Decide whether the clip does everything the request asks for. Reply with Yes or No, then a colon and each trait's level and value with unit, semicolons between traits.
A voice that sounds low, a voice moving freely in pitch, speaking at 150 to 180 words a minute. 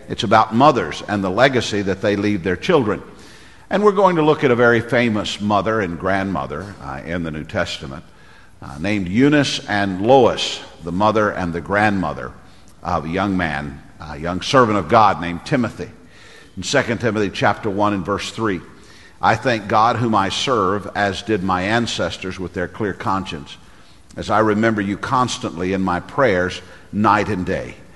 No: low, 100 Hz; average, 3.3 semitones; average, 175 wpm